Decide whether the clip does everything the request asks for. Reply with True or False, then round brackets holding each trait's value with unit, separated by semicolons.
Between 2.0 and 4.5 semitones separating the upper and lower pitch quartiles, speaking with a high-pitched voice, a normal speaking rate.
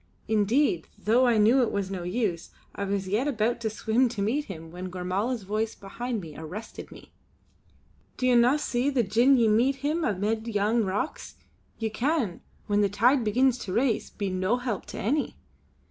True (3.9 semitones; 220 Hz; 185 wpm)